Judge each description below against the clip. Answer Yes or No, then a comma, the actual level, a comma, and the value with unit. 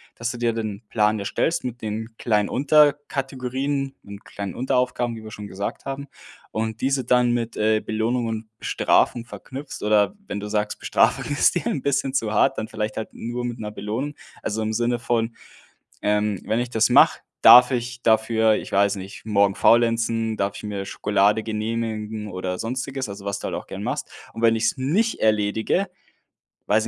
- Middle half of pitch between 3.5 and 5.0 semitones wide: No, average, 2.8 semitones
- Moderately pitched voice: No, low, 115 Hz